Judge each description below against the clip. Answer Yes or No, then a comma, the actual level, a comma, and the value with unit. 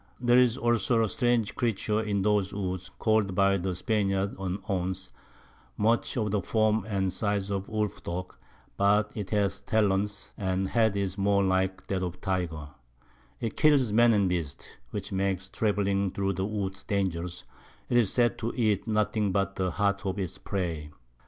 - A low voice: Yes, low, 100 Hz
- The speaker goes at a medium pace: Yes, average, 170 wpm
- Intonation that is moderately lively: No, narrow, 2.3 semitones